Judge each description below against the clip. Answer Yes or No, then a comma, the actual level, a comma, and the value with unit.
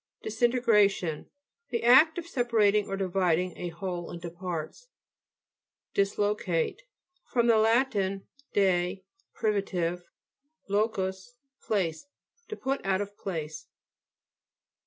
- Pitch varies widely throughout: No, average, 4.4 semitones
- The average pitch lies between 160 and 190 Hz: No, high, 200 Hz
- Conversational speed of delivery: No, slow, 100 wpm